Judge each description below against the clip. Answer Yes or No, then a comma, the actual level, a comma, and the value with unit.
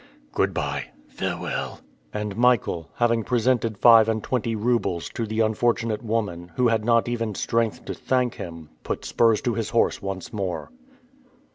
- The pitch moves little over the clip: Yes, narrow, 2.2 semitones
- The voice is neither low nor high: No, low, 115 Hz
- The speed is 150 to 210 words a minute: Yes, average, 155 wpm